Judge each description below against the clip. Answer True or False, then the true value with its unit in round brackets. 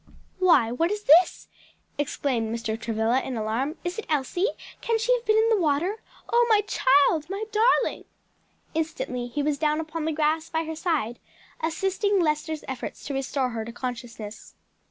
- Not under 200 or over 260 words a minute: False (170 wpm)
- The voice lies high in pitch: True (305 Hz)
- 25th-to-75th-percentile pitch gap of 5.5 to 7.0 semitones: True (6.3 semitones)